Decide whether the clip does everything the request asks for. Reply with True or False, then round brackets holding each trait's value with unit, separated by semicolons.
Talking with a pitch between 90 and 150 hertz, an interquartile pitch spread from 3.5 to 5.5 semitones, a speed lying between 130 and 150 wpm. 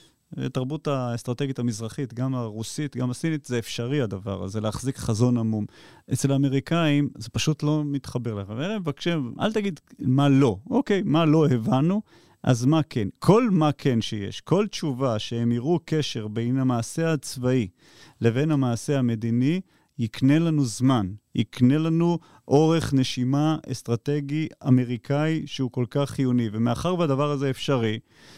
True (135 Hz; 4.2 semitones; 140 wpm)